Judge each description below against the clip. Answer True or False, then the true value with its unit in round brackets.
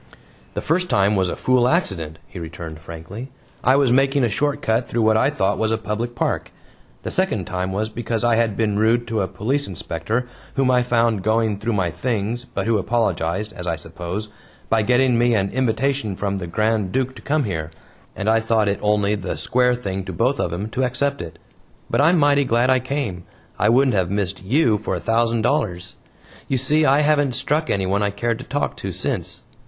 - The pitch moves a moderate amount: True (4.5 semitones)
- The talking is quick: True (210 wpm)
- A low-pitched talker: True (110 Hz)